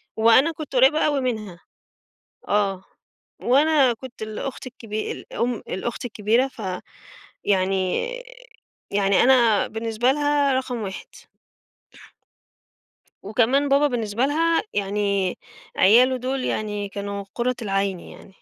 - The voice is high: Yes, high, 230 Hz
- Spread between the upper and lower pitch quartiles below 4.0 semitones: No, average, 4.5 semitones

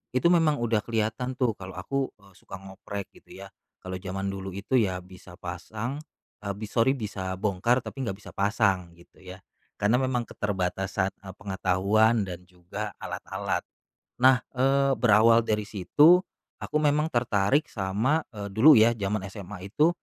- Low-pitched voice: Yes, low, 105 Hz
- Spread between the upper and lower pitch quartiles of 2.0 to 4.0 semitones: No, average, 4.6 semitones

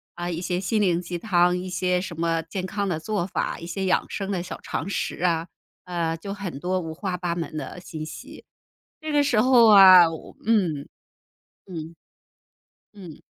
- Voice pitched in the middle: Yes, medium, 180 Hz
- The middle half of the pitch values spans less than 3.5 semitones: Yes, average, 2.7 semitones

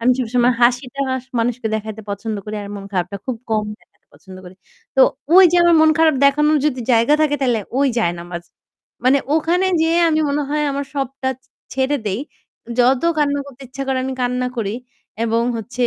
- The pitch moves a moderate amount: Yes, average, 4.2 semitones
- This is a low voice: No, very high, 255 Hz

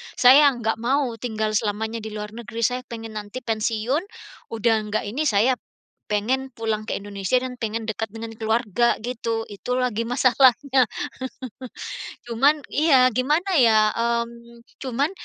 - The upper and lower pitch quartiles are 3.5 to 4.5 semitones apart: No, narrow, 2.6 semitones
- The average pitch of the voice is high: Yes, high, 235 Hz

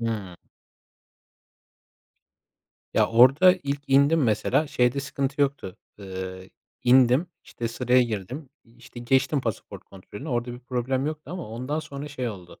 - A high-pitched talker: No, low, 125 Hz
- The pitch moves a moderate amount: Yes, average, 3.5 semitones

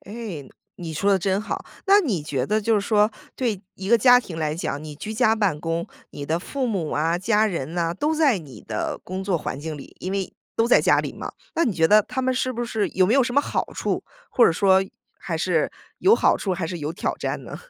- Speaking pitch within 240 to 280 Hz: No, high, 195 Hz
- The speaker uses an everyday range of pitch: No, wide, 5.7 semitones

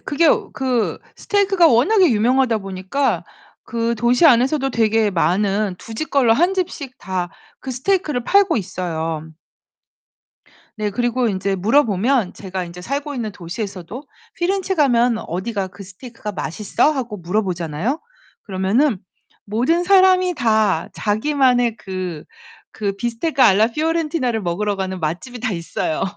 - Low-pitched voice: No, high, 230 Hz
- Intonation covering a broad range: Yes, wide, 6.2 semitones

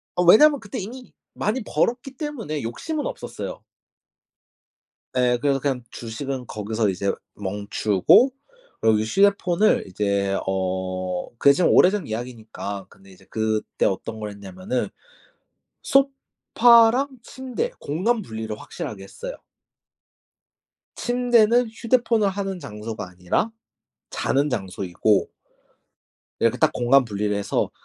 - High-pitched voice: No, low, 125 Hz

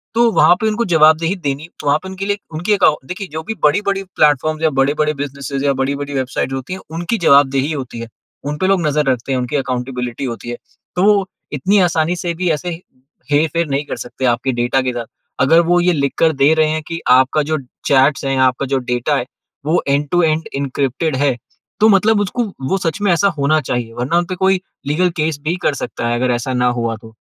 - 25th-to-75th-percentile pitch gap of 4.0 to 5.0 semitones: Yes, average, 4.6 semitones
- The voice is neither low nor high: Yes, medium, 150 Hz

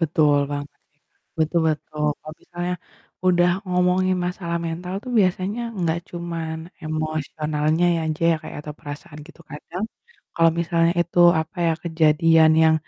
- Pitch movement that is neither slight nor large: No, narrow, 2.1 semitones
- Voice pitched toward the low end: No, medium, 165 Hz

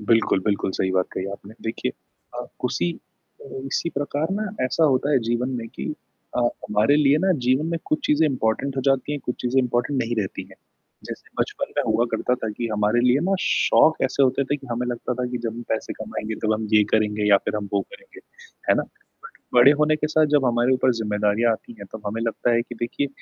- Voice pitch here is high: No, low, 120 Hz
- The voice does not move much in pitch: No, average, 4.1 semitones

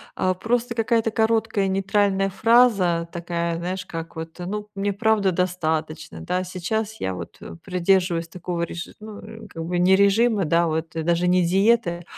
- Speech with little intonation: No, average, 3.7 semitones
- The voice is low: No, medium, 185 Hz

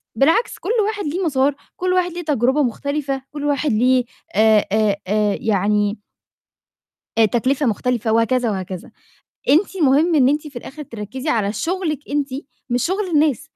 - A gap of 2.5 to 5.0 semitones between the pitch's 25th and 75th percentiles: No, wide, 5.5 semitones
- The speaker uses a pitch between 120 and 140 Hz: No, very high, 265 Hz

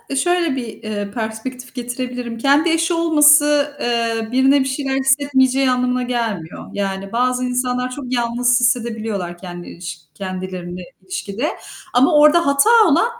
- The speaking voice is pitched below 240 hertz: No, very high, 250 Hz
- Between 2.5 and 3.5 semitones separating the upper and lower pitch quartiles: No, average, 4.0 semitones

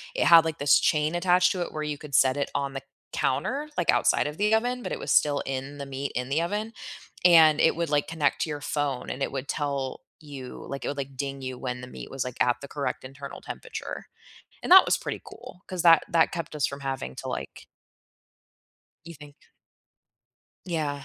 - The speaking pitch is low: No, medium, 145 Hz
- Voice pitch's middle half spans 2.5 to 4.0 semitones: Yes, average, 3.5 semitones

